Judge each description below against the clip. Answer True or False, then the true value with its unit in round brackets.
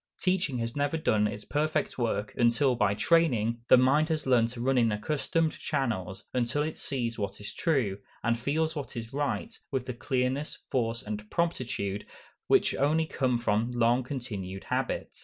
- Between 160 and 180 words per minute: True (170 wpm)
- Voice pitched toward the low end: True (125 Hz)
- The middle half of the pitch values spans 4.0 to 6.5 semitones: True (4.3 semitones)